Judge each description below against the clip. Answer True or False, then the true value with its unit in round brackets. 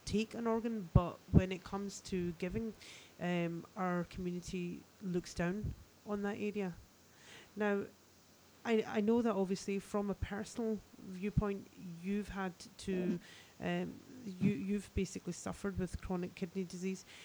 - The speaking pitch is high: True (195 Hz)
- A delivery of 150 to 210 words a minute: False (135 wpm)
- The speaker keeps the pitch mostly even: True (2.3 semitones)